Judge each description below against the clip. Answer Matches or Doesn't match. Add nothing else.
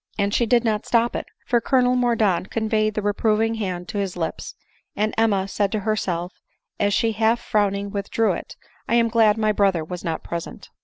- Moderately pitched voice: Doesn't match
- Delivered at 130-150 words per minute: Doesn't match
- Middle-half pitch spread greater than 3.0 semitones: Doesn't match